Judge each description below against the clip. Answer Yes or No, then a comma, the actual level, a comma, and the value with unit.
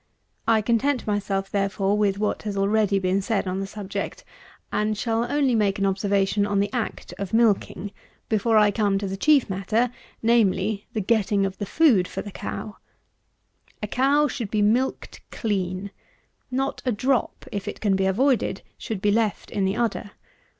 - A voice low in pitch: No, high, 205 Hz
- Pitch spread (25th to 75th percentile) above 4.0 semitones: No, average, 2.7 semitones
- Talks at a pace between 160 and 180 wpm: Yes, average, 175 wpm